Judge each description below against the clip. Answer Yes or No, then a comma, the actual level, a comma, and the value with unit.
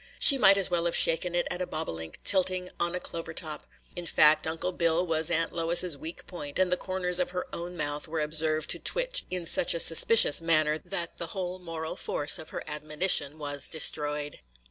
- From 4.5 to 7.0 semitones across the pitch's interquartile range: No, average, 2.7 semitones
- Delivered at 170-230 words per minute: Yes, fast, 205 wpm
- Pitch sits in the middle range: Yes, medium, 165 Hz